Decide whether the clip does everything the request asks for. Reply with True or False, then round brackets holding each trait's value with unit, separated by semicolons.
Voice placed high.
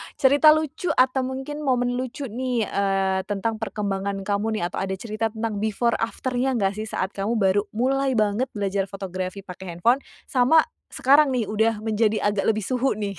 True (220 Hz)